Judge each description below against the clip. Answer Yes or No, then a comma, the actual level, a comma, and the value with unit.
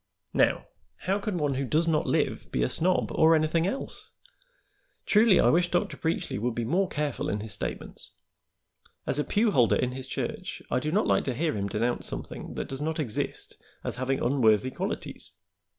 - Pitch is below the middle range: No, medium, 150 Hz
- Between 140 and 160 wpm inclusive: No, average, 190 wpm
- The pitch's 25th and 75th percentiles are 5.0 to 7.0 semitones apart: Yes, wide, 5.5 semitones